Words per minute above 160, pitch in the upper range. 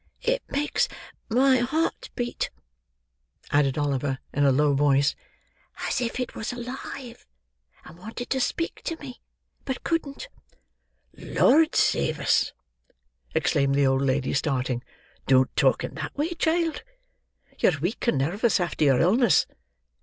No: slow, 135 wpm; high, 215 Hz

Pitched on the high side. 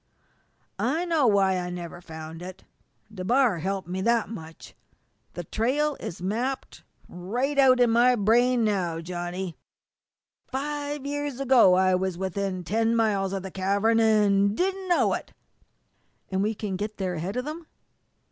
Yes: high, 205 Hz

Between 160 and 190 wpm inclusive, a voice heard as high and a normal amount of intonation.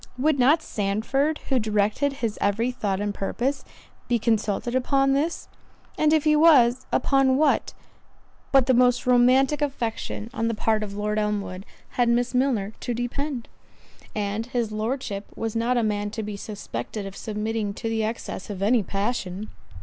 Yes: average, 165 wpm; high, 230 Hz; average, 3.8 semitones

